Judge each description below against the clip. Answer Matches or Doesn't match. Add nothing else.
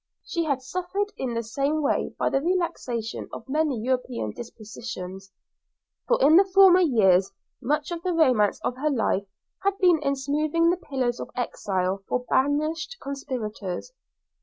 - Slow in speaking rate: Doesn't match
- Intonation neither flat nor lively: Doesn't match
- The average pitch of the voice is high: Matches